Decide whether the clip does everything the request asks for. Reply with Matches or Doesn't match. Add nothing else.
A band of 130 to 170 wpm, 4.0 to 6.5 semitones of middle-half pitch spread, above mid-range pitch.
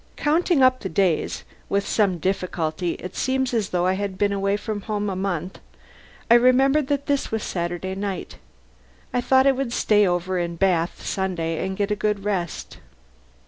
Doesn't match